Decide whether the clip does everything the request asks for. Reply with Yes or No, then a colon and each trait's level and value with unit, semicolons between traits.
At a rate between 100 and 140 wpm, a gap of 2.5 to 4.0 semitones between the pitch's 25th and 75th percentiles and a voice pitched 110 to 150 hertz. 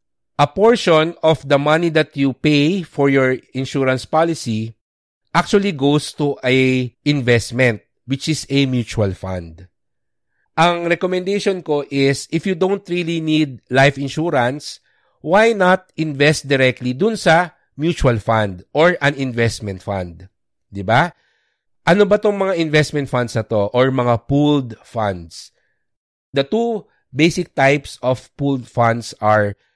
No: slow, 135 wpm; wide, 5.4 semitones; medium, 140 Hz